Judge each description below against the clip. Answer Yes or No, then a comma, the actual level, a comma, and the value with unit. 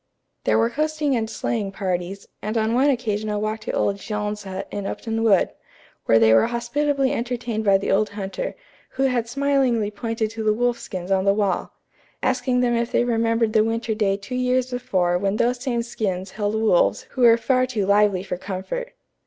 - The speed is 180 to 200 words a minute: Yes, average, 195 wpm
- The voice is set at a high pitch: Yes, high, 220 Hz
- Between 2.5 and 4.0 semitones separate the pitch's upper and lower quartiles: Yes, average, 3.5 semitones